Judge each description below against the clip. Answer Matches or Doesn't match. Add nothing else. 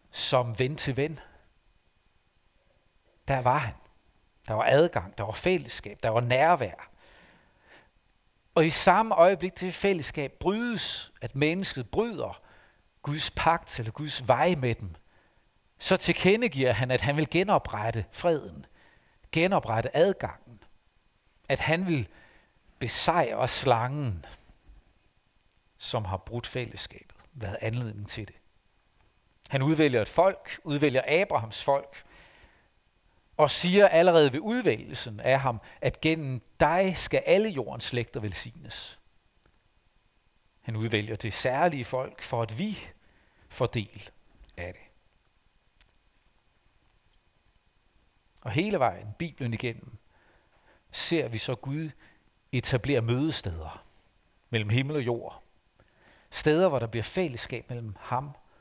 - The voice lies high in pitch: Doesn't match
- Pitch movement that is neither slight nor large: Doesn't match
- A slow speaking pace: Matches